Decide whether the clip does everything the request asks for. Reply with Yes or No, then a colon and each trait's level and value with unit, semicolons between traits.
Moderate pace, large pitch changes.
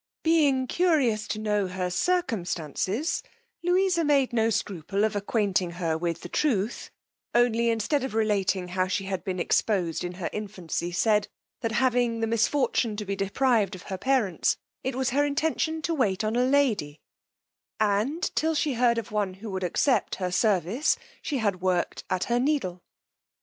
Yes: average, 165 wpm; wide, 5.8 semitones